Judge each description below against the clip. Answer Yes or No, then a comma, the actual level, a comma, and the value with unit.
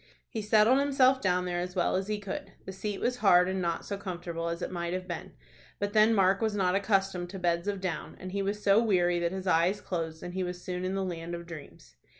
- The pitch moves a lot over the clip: No, narrow, 2.5 semitones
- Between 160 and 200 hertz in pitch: Yes, medium, 185 Hz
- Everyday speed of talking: No, fast, 250 wpm